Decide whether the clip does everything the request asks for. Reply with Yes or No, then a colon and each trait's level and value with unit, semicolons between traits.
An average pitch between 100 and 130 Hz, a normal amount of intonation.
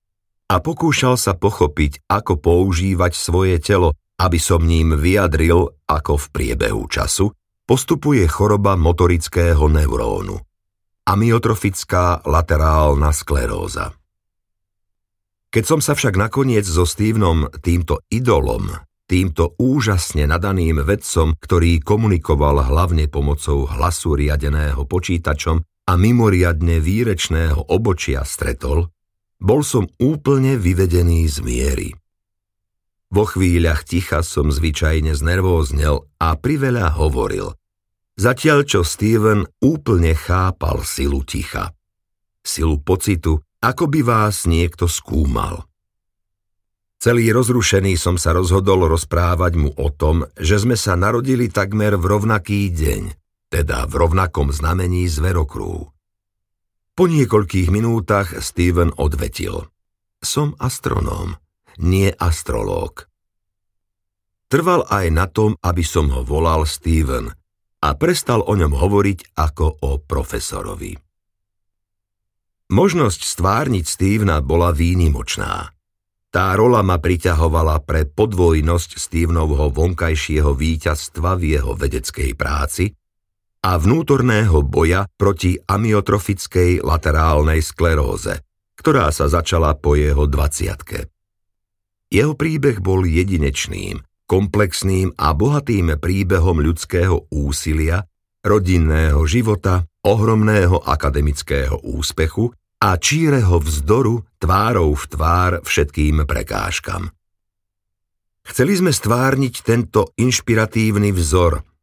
No: very low, 90 Hz; average, 4.0 semitones